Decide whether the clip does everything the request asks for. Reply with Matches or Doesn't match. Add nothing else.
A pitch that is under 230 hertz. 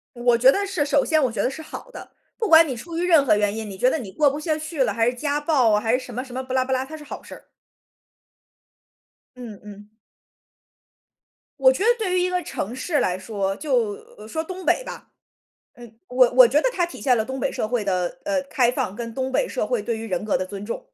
Doesn't match